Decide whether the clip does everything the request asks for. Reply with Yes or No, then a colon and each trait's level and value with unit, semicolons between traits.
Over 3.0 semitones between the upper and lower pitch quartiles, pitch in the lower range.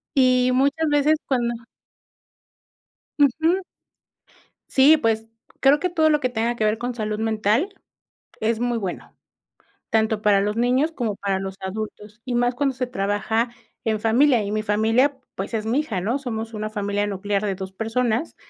No: average, 3.6 semitones; high, 225 Hz